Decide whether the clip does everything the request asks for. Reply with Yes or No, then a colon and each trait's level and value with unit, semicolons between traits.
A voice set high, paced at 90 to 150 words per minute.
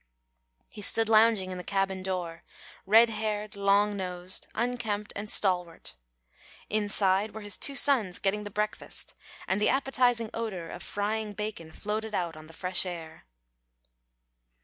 Yes: high, 205 Hz; average, 145 wpm